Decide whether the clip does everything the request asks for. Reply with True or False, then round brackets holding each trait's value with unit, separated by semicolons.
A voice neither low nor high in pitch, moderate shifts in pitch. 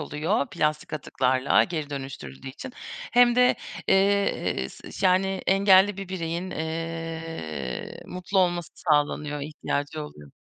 True (165 Hz; 4.6 semitones)